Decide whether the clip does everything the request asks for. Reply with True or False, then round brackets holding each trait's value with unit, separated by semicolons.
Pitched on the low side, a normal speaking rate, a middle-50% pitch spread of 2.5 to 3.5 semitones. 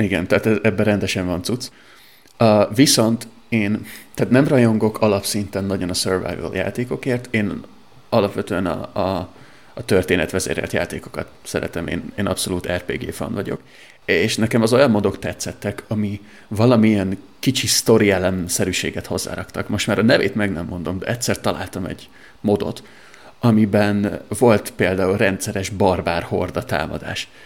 True (105 Hz; 135 wpm; 2.9 semitones)